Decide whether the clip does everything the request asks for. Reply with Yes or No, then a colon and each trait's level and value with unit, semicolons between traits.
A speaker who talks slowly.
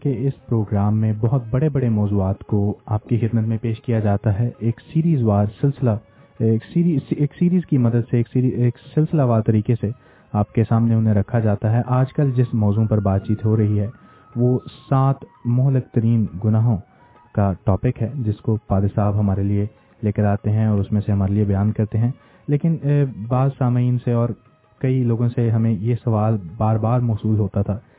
No: fast, 205 wpm